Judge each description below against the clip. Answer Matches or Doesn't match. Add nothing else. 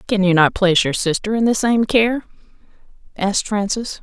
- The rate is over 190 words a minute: Doesn't match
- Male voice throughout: Doesn't match